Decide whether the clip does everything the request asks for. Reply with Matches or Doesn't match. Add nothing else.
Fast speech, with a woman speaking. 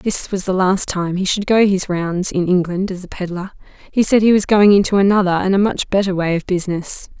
Matches